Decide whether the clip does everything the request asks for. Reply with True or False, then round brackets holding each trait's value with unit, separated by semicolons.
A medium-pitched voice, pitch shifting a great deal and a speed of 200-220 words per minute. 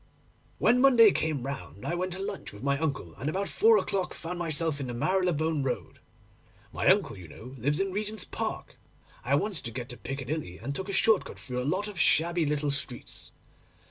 True (155 Hz; 5.7 semitones; 205 wpm)